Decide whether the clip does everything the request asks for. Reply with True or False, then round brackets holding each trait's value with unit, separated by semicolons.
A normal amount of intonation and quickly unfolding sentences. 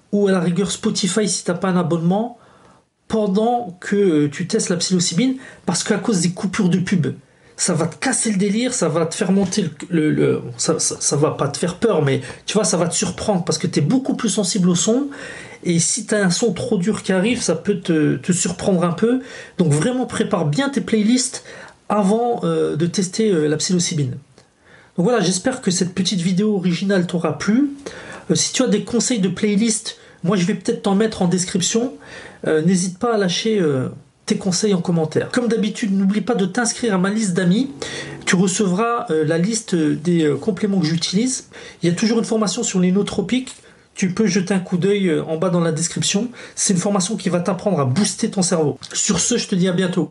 True (4.0 semitones; 225 wpm)